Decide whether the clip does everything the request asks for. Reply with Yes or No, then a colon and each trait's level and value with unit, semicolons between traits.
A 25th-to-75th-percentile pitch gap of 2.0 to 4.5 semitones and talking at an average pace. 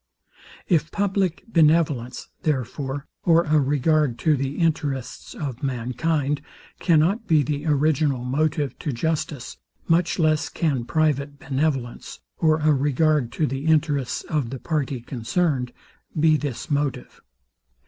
No: average, 2.9 semitones; slow, 125 wpm